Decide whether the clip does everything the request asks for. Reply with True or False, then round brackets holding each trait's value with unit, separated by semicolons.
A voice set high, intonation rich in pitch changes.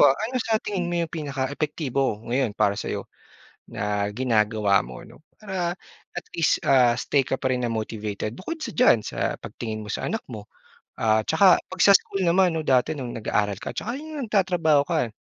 False (135 Hz; 8.5 semitones)